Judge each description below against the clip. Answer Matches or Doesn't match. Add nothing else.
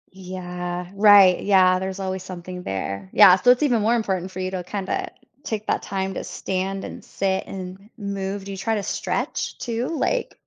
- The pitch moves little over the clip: Matches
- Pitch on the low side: Doesn't match